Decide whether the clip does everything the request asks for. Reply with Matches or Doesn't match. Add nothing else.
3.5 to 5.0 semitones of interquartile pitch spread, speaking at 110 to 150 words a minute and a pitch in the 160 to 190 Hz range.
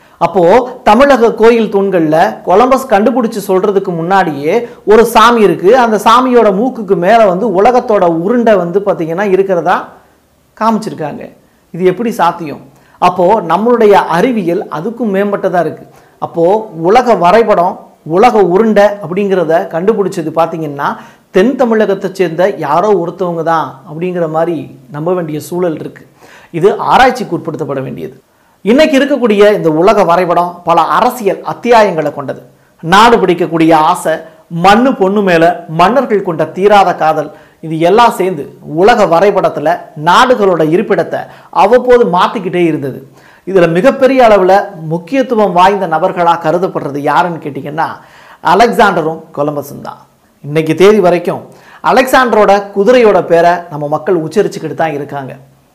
Matches